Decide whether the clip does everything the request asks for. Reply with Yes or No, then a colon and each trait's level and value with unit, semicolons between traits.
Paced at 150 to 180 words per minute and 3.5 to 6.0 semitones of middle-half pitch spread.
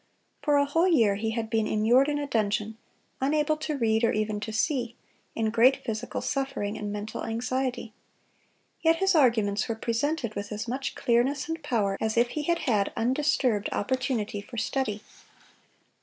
Yes: average, 170 wpm; average, 4.4 semitones